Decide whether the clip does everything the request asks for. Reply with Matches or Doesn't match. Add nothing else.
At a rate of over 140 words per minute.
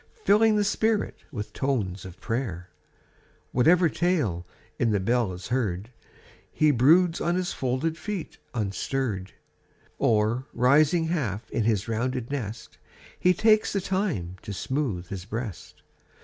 Doesn't match